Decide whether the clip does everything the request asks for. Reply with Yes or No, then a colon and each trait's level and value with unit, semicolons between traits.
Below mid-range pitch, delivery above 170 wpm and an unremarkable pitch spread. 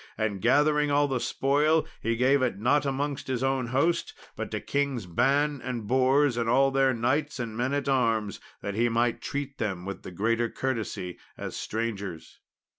Yes: low, 130 Hz; average, 180 wpm; average, 3.7 semitones